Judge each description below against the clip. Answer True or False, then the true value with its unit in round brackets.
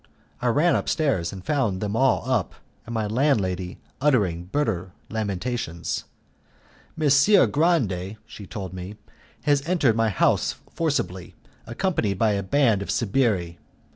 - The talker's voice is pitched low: True (110 Hz)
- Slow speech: True (130 wpm)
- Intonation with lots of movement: True (6.9 semitones)